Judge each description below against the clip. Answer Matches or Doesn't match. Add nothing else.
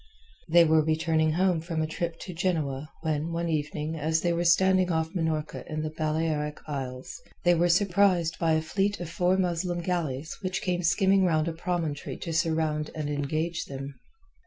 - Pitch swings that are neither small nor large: Doesn't match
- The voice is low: Doesn't match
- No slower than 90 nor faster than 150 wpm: Doesn't match